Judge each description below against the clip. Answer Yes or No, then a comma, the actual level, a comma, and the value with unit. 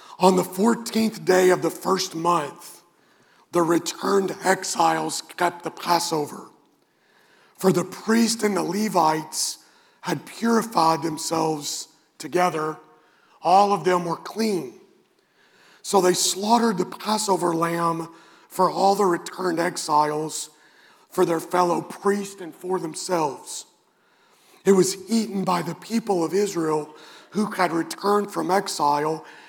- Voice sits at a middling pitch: Yes, medium, 180 Hz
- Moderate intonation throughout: Yes, average, 3.4 semitones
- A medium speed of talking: No, slow, 120 wpm